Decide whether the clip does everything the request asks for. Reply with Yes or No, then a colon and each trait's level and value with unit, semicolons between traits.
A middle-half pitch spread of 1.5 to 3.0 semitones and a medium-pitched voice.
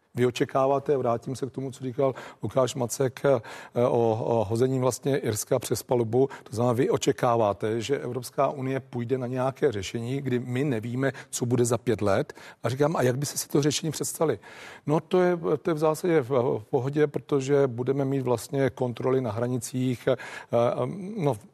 No: narrow, 2.5 semitones; low, 130 Hz